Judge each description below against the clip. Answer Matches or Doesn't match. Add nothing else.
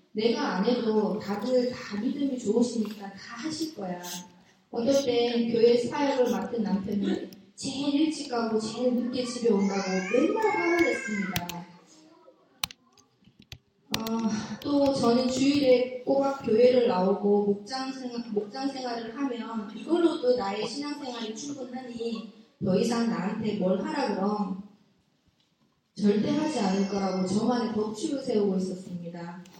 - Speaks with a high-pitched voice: Matches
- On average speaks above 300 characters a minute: Doesn't match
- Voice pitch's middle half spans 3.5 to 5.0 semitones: Matches